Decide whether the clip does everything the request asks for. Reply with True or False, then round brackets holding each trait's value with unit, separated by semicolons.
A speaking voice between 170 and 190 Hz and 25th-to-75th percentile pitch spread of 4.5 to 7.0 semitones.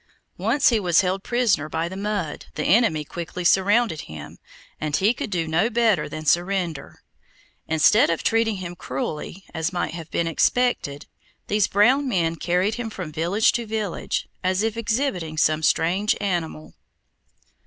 True (185 Hz; 5.1 semitones)